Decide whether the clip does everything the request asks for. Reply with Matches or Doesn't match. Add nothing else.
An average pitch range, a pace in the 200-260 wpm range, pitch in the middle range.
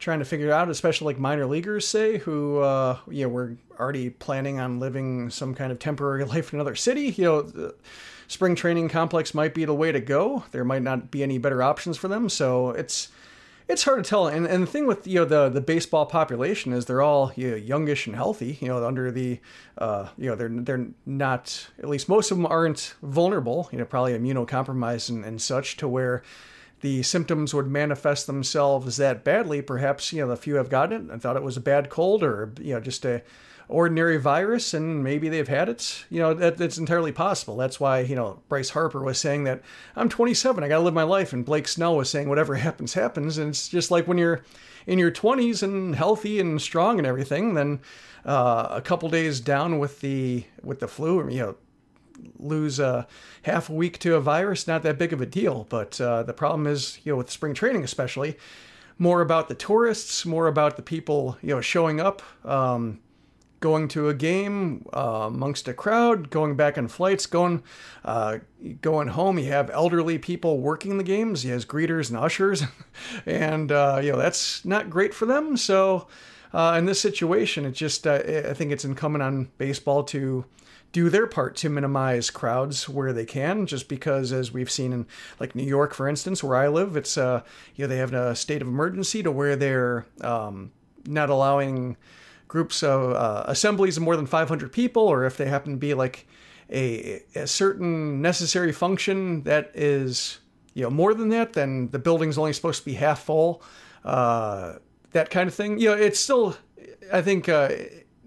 Matches